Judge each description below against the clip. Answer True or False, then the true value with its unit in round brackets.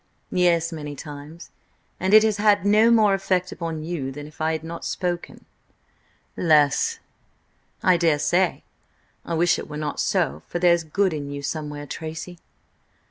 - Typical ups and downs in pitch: True (3.5 semitones)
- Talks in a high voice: False (165 Hz)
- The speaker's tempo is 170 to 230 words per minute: False (150 wpm)